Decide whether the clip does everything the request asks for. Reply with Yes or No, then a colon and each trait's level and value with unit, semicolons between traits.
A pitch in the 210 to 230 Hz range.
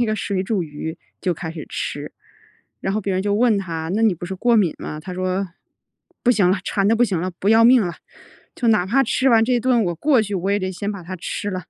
No: high, 200 Hz